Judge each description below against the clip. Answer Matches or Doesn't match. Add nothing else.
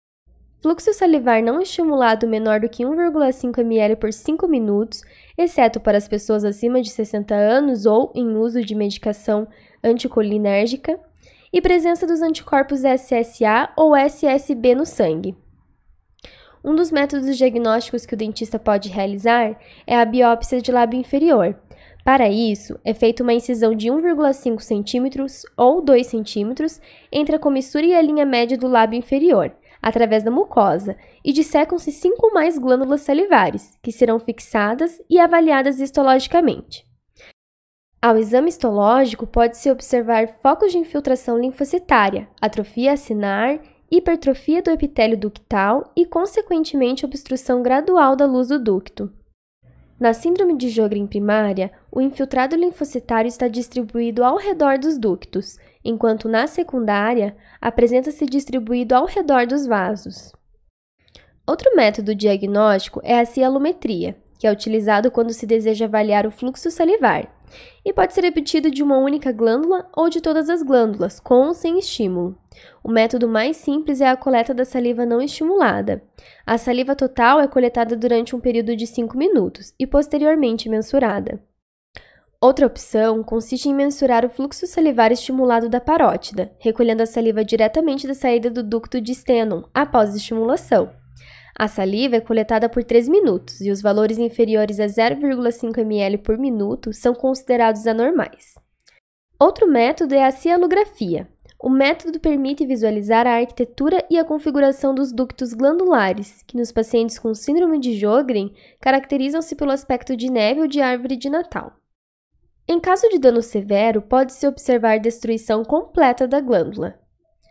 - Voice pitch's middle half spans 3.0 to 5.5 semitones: Matches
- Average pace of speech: Matches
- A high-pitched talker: Matches